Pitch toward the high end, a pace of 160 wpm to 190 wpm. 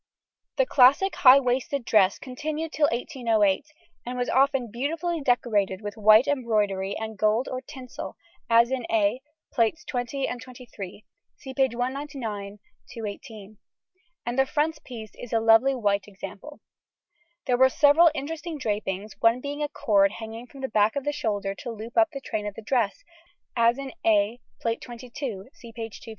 Yes: high, 240 Hz; average, 165 wpm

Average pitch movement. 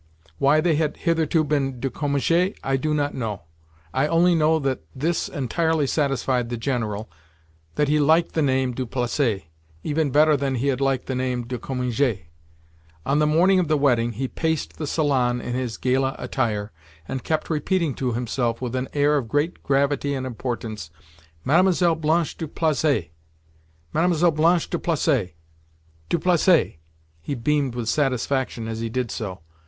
Yes: average, 4.0 semitones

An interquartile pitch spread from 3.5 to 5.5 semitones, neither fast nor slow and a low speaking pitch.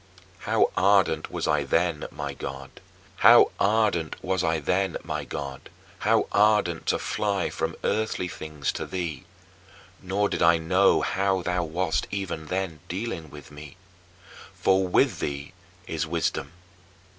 No: average, 3.8 semitones; slow, 120 wpm; very low, 85 Hz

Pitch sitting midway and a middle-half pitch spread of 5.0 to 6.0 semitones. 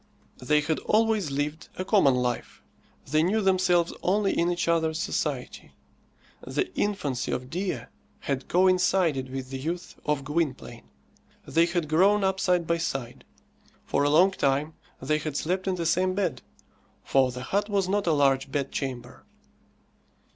Yes: medium, 165 Hz; average, 5.3 semitones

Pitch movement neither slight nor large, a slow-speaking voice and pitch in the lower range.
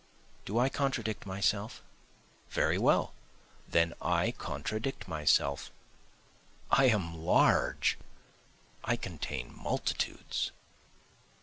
No: wide, 5.9 semitones; slow, 85 wpm; low, 100 Hz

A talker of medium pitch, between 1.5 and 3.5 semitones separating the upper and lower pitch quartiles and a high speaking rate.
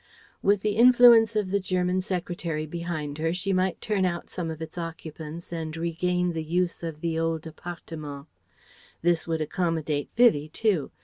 No: medium, 170 Hz; narrow, 2.5 semitones; average, 165 wpm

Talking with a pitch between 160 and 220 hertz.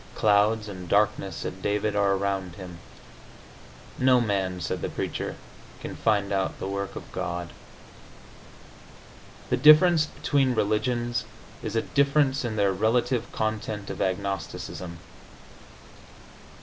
No: low, 105 Hz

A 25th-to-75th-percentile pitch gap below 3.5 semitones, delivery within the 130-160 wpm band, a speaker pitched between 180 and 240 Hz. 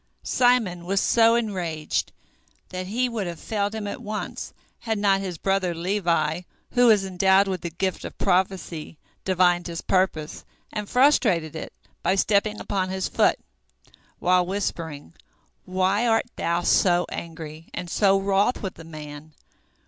Yes: average, 3.1 semitones; average, 150 wpm; high, 190 Hz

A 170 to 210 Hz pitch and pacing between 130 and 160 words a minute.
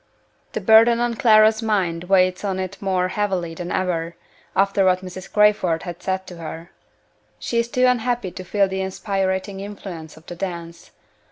No: high, 190 Hz; average, 170 wpm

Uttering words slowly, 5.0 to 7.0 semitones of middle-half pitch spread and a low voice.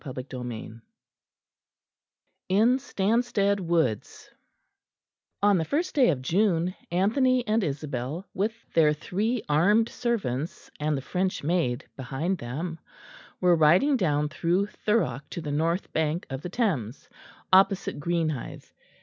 No: slow, 125 wpm; wide, 5.6 semitones; medium, 170 Hz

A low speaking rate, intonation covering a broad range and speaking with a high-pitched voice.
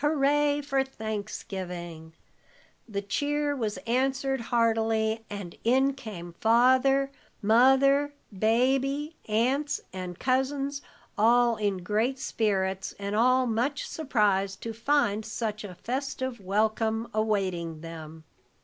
No: slow, 105 wpm; average, 5.0 semitones; high, 225 Hz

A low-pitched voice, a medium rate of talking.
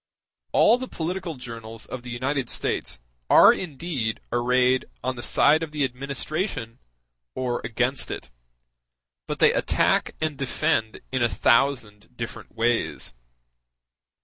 No: low, 130 Hz; slow, 125 wpm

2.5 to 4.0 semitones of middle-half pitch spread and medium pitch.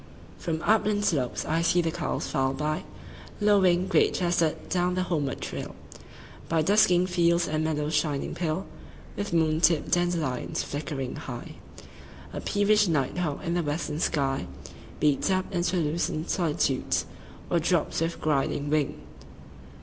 Yes: average, 3.1 semitones; medium, 165 Hz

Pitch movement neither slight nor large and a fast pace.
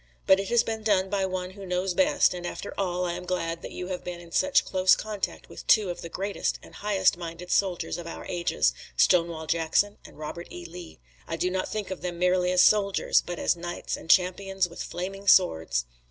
No: narrow, 2.1 semitones; fast, 220 wpm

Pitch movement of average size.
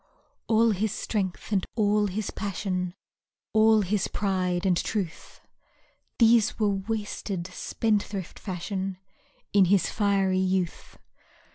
No: narrow, 2.3 semitones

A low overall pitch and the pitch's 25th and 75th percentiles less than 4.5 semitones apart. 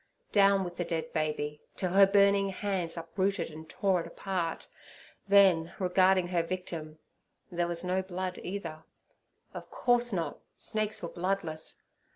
No: medium, 180 Hz; average, 2.9 semitones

